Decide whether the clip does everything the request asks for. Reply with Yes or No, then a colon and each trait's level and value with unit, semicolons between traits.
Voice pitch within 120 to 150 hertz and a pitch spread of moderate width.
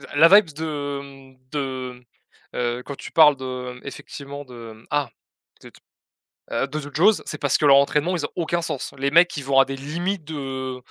Yes: medium, 140 Hz; average, 3.0 semitones